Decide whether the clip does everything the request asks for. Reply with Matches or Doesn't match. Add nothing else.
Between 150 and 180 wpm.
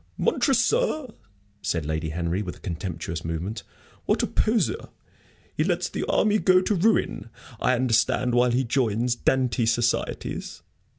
Doesn't match